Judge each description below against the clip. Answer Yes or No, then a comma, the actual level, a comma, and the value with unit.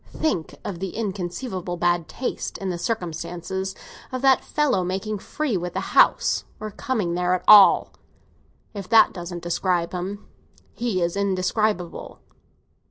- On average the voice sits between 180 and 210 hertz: Yes, high, 190 Hz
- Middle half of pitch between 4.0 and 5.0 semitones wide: No, average, 3.4 semitones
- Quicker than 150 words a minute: No, slow, 135 wpm